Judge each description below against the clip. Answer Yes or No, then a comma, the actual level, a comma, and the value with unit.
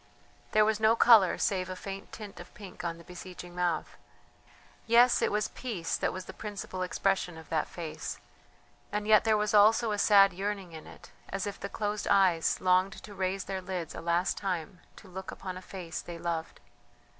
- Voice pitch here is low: No, high, 190 Hz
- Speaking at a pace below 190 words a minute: No, average, 195 wpm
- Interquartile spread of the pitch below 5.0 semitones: Yes, average, 2.7 semitones